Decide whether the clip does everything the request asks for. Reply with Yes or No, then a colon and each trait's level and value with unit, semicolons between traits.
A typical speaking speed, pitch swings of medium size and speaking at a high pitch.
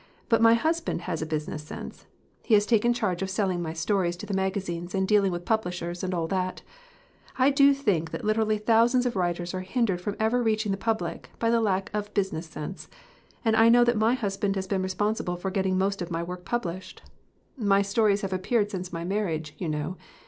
No: fast, 215 wpm; average, 3.7 semitones; high, 195 Hz